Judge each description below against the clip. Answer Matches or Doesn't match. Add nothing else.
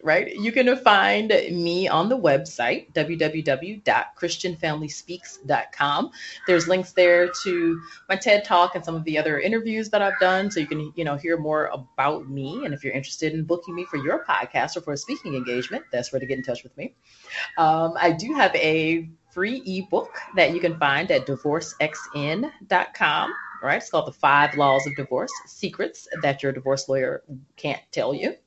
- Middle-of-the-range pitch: Matches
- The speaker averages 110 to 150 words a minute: Doesn't match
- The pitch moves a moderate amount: Matches